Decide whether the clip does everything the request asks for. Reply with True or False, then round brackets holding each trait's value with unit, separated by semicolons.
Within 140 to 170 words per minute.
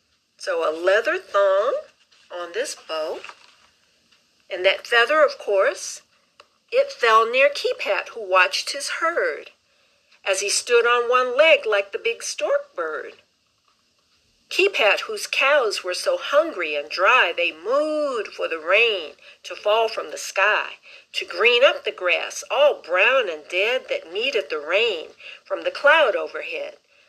True (145 wpm)